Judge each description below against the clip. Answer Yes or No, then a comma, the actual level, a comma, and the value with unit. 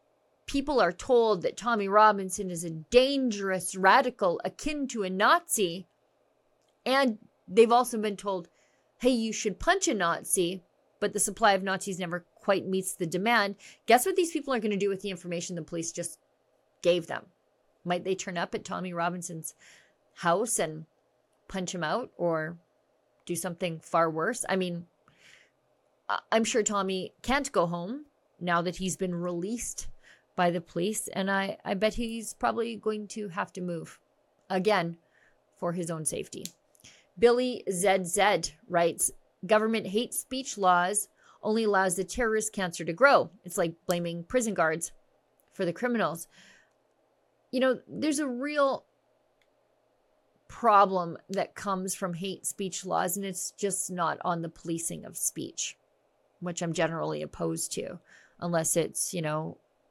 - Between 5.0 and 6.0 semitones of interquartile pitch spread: No, average, 4.3 semitones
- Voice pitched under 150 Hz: No, high, 190 Hz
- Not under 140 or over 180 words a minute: Yes, average, 150 wpm